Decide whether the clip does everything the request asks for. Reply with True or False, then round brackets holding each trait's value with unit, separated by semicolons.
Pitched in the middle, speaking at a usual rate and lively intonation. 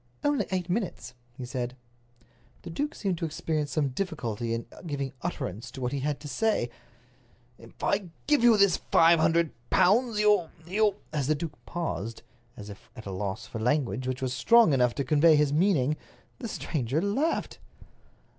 True (155 Hz; 170 wpm; 6.8 semitones)